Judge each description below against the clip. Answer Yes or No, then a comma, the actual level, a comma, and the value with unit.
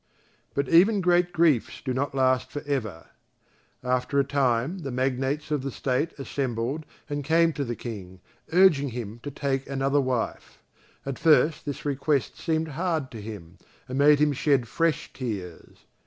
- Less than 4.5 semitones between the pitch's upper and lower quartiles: Yes, average, 3.2 semitones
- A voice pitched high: No, medium, 140 Hz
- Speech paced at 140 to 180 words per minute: Yes, average, 160 wpm